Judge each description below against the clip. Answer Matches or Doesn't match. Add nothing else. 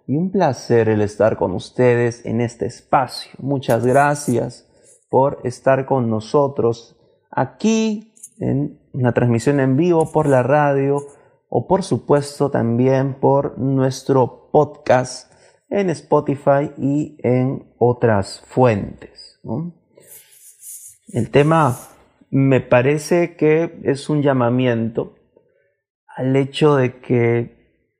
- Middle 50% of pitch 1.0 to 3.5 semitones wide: Matches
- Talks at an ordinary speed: Doesn't match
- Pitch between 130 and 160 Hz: Matches